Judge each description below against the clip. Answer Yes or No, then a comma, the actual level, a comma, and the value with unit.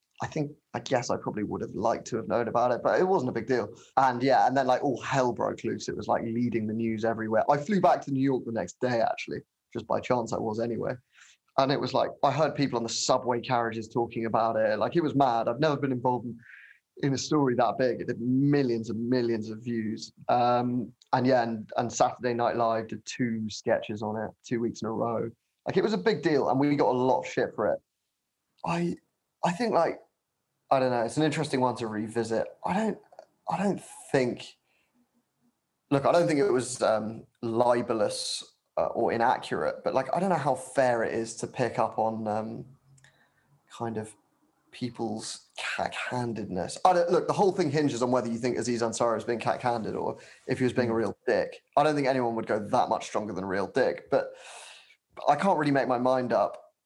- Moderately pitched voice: No, low, 125 Hz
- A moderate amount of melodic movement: Yes, average, 3.8 semitones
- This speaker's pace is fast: Yes, fast, 225 wpm